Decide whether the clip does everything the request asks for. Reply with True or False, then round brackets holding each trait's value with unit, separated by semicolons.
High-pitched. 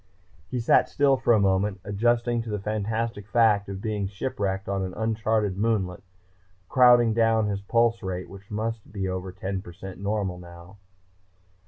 False (105 Hz)